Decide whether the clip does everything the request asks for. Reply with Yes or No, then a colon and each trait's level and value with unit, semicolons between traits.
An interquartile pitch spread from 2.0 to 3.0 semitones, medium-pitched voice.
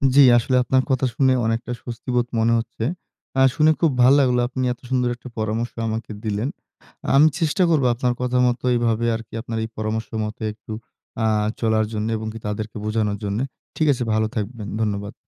No: narrow, 2.5 semitones; low, 115 Hz